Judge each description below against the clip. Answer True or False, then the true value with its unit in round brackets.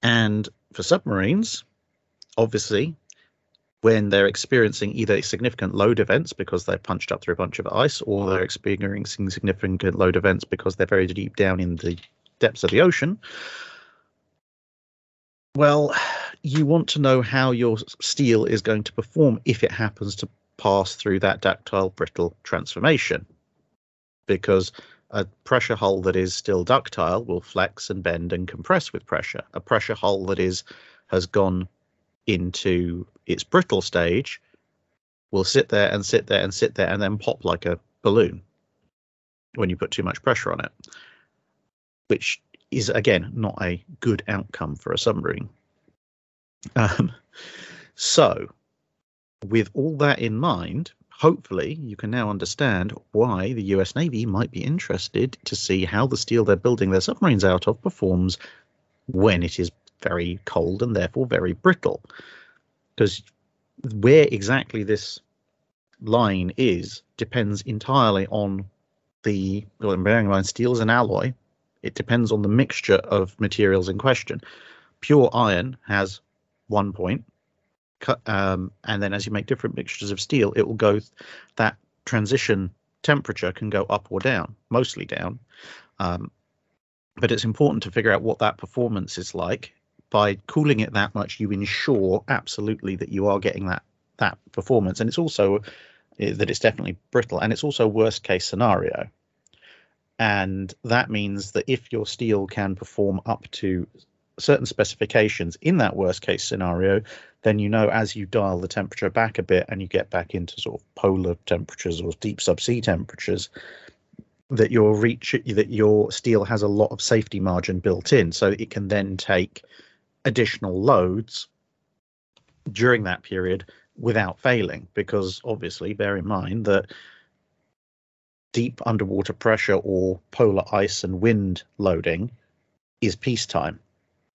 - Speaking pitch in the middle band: False (105 Hz)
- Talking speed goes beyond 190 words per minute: False (155 wpm)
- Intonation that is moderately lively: True (3.6 semitones)